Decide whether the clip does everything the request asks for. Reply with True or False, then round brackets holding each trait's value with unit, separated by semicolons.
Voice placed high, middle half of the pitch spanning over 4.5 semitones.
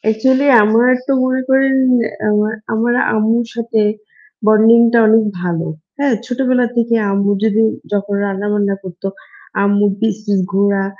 False (220 Hz; 2.8 semitones)